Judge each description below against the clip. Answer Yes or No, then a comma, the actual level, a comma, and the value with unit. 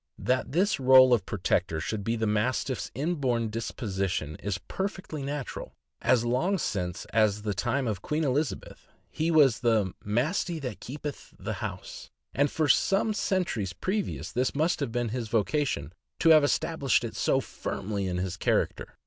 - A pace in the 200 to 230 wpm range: No, average, 160 wpm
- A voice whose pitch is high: No, low, 125 Hz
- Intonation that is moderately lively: No, wide, 6.2 semitones